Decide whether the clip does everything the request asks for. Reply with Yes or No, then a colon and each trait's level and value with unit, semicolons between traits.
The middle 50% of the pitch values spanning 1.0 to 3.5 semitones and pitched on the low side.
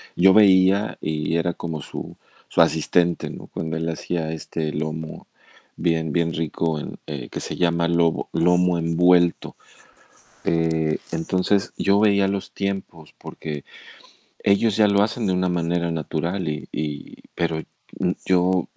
Yes: narrow, 2.5 semitones; very low, 85 Hz